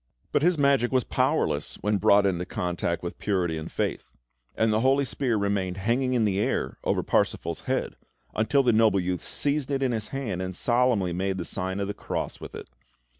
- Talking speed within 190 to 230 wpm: Yes, average, 200 wpm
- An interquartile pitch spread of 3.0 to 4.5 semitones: No, wide, 5.4 semitones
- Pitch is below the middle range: Yes, low, 105 Hz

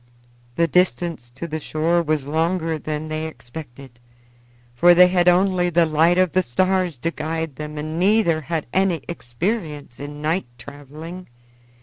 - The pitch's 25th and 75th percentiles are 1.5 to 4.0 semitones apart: Yes, average, 2.9 semitones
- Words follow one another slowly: No, average, 150 wpm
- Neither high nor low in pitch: Yes, medium, 160 Hz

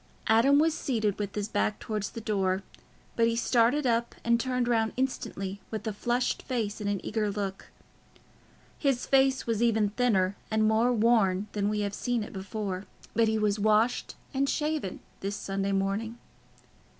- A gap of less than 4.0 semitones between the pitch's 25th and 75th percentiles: Yes, average, 2.9 semitones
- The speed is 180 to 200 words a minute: No, average, 170 wpm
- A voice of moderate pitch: No, high, 220 Hz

